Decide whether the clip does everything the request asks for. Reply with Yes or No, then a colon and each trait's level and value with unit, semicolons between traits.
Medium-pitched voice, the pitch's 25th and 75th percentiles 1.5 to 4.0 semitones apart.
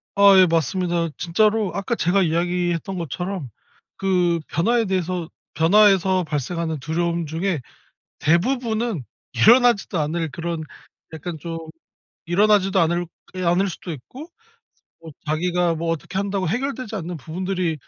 Yes: medium, 175 Hz; average, 3.0 semitones